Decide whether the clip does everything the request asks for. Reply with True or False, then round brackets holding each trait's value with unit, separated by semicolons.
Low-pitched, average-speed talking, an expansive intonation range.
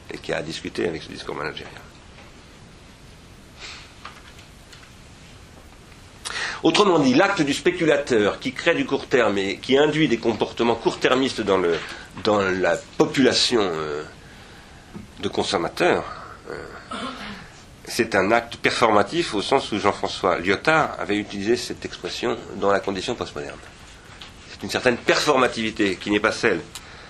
False (115 Hz; 130 wpm; 7.0 semitones)